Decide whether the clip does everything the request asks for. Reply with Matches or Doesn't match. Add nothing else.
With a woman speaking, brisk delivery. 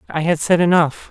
Doesn't match